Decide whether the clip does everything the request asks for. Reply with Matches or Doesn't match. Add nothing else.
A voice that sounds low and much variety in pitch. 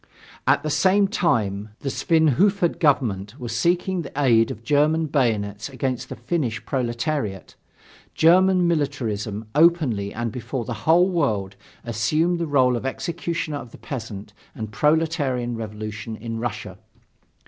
Matches